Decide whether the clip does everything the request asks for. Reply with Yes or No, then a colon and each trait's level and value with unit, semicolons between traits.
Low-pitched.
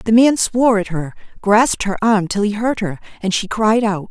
No: high, 210 Hz